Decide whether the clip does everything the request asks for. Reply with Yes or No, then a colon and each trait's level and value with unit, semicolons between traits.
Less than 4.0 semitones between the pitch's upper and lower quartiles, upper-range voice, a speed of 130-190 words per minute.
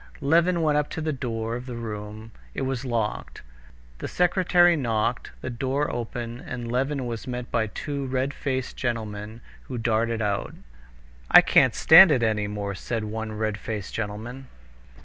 No: average, 3.5 semitones; low, 120 Hz; average, 170 wpm